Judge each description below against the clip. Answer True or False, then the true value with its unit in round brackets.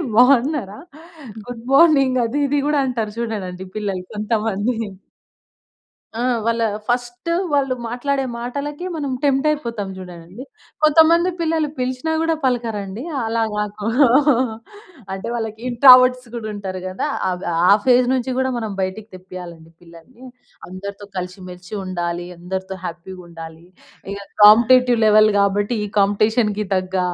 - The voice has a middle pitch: False (220 Hz)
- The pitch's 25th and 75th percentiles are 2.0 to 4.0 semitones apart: False (5.1 semitones)